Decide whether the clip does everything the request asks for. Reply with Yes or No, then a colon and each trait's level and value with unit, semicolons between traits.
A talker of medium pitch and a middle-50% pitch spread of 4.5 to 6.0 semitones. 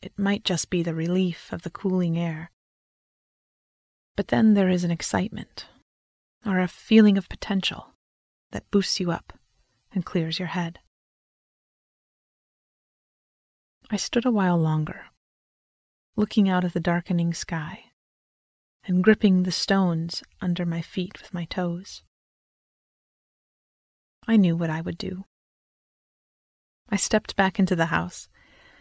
No: medium, 180 Hz; average, 2.8 semitones